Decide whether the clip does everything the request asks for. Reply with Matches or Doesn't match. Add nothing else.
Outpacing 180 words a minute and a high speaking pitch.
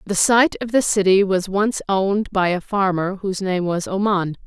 Matches